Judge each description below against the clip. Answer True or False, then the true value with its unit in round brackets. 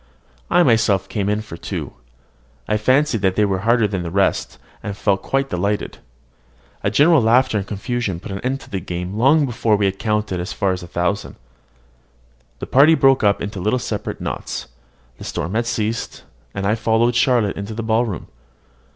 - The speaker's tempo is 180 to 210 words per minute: True (185 wpm)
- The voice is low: True (105 Hz)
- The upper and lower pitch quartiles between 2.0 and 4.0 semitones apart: True (3.5 semitones)